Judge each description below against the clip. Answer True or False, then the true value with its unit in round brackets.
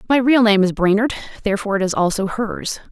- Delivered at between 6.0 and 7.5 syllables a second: True (6.4 syllables/s)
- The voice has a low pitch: False (210 Hz)